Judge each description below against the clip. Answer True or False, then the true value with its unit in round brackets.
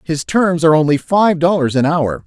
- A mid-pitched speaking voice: True (160 Hz)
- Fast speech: True (210 wpm)